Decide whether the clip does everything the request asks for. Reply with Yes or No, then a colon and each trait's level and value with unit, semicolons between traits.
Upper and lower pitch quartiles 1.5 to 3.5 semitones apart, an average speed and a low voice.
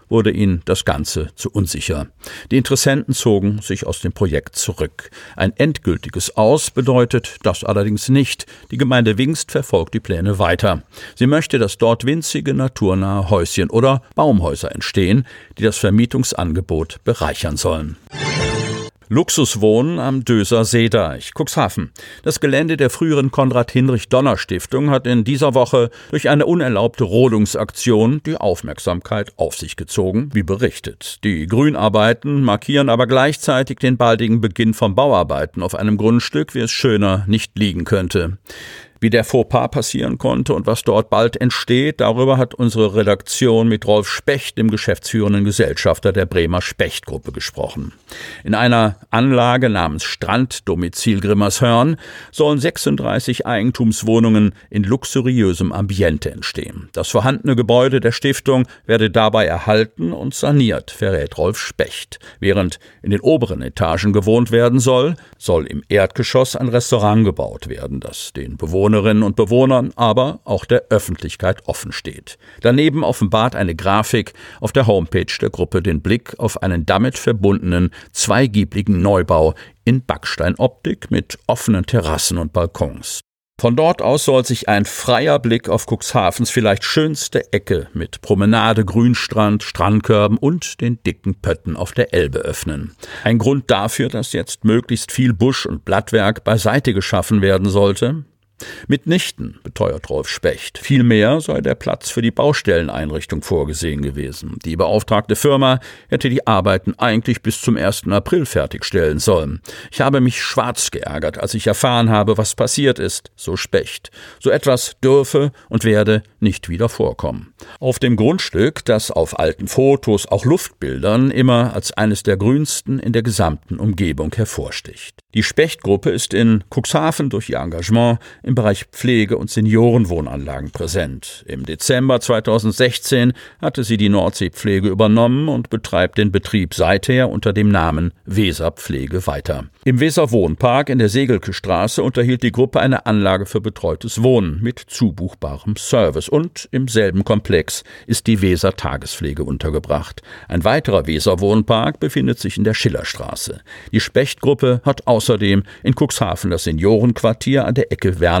No: average, 4.3 semitones; average, 140 wpm; low, 110 Hz